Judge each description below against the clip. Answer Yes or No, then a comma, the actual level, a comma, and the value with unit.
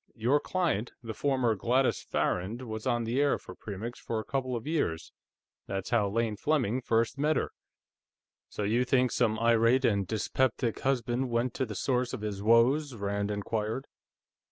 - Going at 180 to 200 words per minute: No, average, 170 wpm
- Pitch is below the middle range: Yes, low, 115 Hz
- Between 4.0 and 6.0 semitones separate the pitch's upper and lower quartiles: No, average, 3.2 semitones